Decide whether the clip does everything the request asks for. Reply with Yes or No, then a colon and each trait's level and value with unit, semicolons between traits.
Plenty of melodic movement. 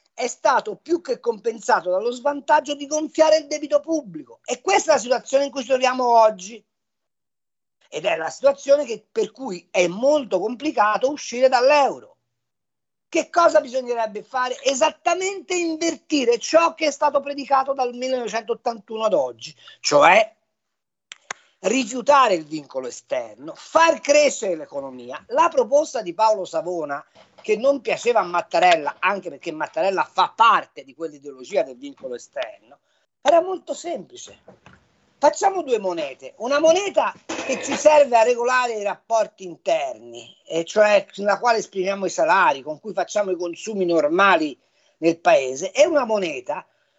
Yes: wide, 6.8 semitones